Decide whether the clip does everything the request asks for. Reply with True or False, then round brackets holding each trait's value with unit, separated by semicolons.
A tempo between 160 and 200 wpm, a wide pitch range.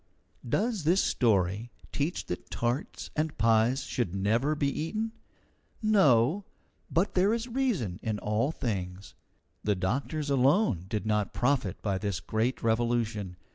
False (135 wpm; 6.8 semitones)